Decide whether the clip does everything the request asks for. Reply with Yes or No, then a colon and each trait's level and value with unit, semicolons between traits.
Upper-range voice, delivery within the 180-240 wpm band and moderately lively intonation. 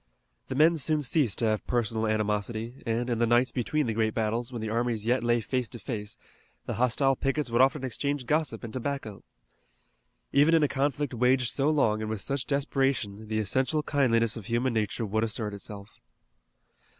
No: low, 120 Hz; average, 185 wpm; average, 3.6 semitones